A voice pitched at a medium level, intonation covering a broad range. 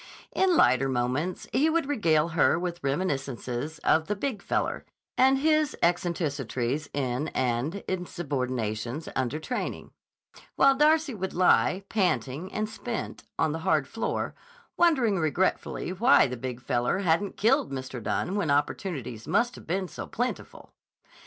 Yes: medium, 170 Hz; wide, 8.0 semitones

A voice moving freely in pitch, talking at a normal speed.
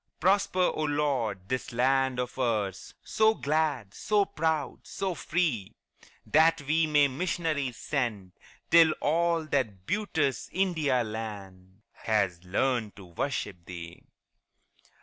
No: wide, 7.2 semitones; slow, 115 wpm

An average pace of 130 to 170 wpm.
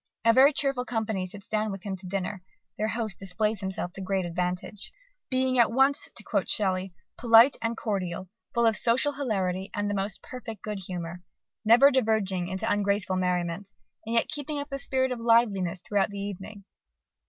No: average, 180 wpm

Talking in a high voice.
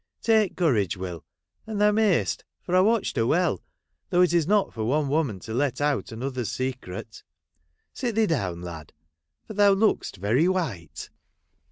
No: medium, 145 Hz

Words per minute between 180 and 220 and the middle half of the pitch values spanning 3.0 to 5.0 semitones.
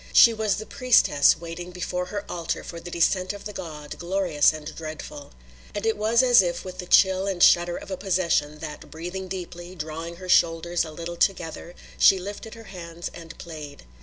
No: average, 195 wpm; narrow, 2.6 semitones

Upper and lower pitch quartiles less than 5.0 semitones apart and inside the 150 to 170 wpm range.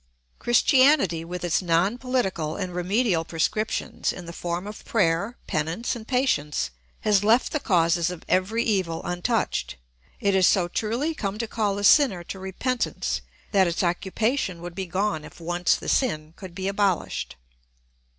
Yes: average, 4.4 semitones; average, 160 wpm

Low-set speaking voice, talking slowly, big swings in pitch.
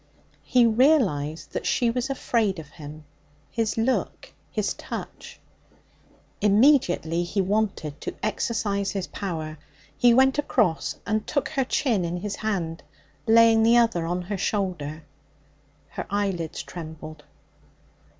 No: high, 200 Hz; slow, 125 wpm; wide, 5.7 semitones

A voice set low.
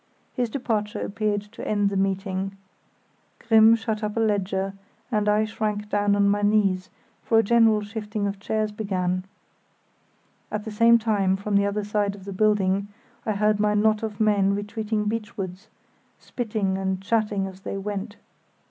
No: high, 210 Hz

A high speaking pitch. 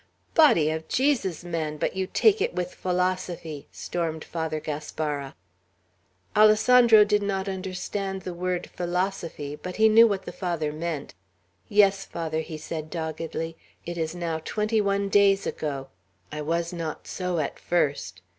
No: medium, 175 Hz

